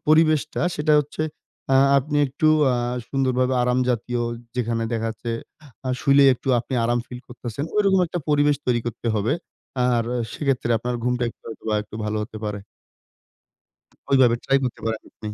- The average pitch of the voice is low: Yes, low, 125 Hz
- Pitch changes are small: No, average, 3.3 semitones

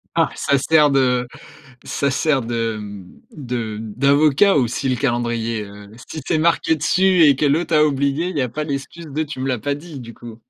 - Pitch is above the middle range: No, medium, 140 Hz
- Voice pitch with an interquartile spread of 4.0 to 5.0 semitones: Yes, average, 4.5 semitones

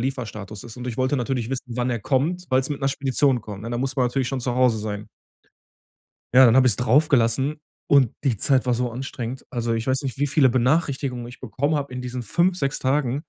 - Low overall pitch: Yes, low, 130 Hz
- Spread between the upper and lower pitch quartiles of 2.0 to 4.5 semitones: Yes, narrow, 2.4 semitones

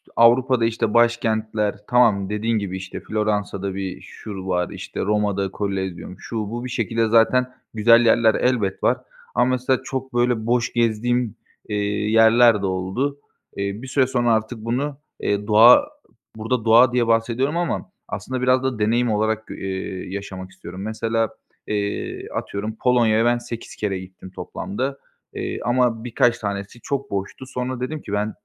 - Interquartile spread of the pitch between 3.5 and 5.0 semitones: No, average, 3.1 semitones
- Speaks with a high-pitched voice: No, low, 115 Hz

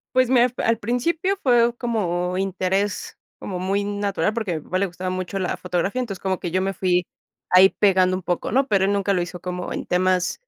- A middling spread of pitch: Yes, average, 3.0 semitones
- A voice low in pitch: No, high, 190 Hz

